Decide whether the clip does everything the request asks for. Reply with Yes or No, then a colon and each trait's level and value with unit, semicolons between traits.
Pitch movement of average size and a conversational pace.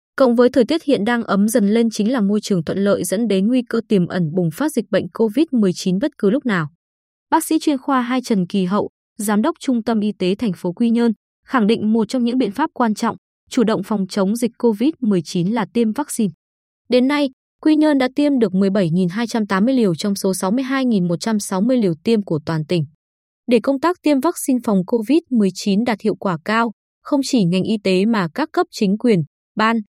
Yes: average, 4.5 semitones; average, 210 wpm